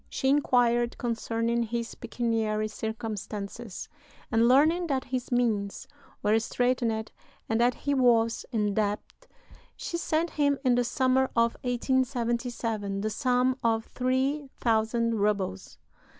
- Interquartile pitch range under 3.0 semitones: Yes, narrow, 2.6 semitones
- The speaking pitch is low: No, high, 235 Hz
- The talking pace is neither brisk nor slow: No, slow, 120 wpm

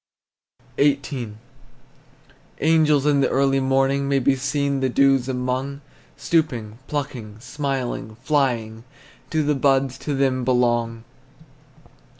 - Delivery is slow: Yes, slow, 110 wpm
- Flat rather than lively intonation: Yes, narrow, 2.2 semitones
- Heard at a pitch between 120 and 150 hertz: Yes, low, 135 Hz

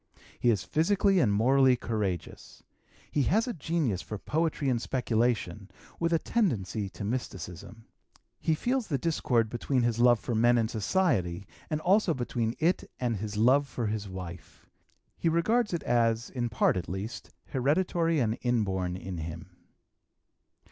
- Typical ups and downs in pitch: No, wide, 7.1 semitones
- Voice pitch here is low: Yes, low, 120 Hz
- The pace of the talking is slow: No, average, 150 wpm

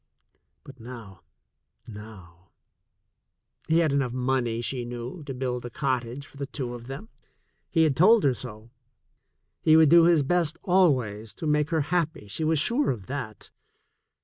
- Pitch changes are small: No, average, 5.0 semitones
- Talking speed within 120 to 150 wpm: No, average, 160 wpm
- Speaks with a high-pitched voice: No, low, 135 Hz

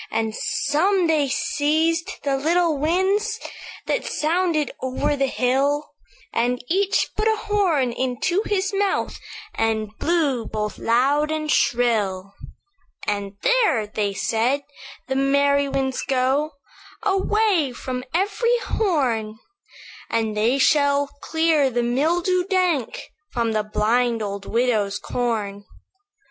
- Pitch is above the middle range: Yes, very high, 275 Hz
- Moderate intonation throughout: No, wide, 6.5 semitones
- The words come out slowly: Yes, slow, 115 wpm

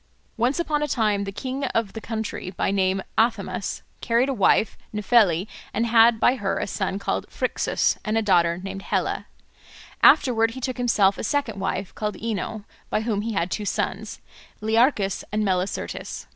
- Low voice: No, high, 215 Hz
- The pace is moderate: Yes, average, 175 wpm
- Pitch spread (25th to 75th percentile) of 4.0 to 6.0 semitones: No, average, 3.0 semitones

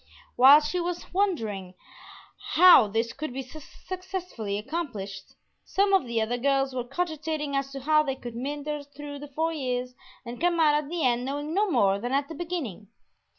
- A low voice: No, very high, 280 Hz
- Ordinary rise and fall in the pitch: Yes, average, 4.8 semitones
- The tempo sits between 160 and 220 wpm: Yes, average, 180 wpm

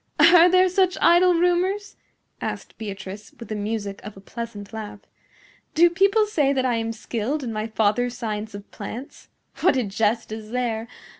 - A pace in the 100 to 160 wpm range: No, average, 170 wpm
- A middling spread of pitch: No, wide, 8.0 semitones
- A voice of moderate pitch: No, high, 230 Hz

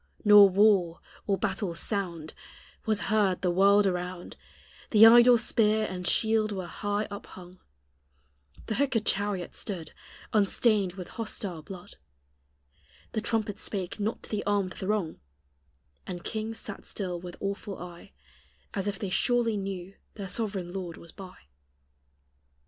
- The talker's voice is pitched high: Yes, high, 200 Hz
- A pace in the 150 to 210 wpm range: No, average, 140 wpm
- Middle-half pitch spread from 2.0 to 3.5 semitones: Yes, average, 2.9 semitones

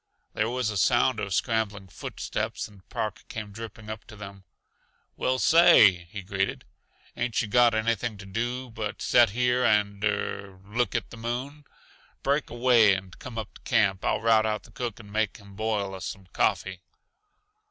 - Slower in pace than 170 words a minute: No, average, 180 wpm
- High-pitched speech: No, low, 110 Hz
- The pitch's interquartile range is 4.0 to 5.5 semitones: No, average, 3.1 semitones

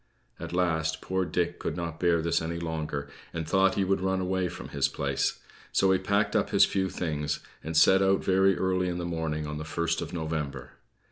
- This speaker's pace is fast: Yes, fast, 210 wpm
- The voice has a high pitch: No, very low, 85 Hz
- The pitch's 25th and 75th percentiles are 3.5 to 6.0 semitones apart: No, average, 2.8 semitones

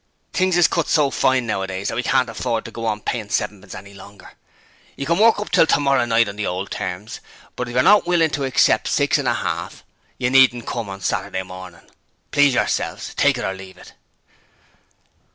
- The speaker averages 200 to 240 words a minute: Yes, fast, 205 wpm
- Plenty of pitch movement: Yes, wide, 5.8 semitones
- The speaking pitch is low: Yes, low, 115 Hz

